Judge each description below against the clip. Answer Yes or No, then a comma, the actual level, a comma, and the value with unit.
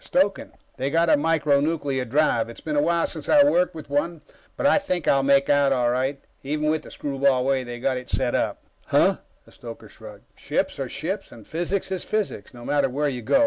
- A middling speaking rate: No, fast, 225 wpm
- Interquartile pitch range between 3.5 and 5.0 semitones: Yes, average, 3.8 semitones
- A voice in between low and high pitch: Yes, medium, 145 Hz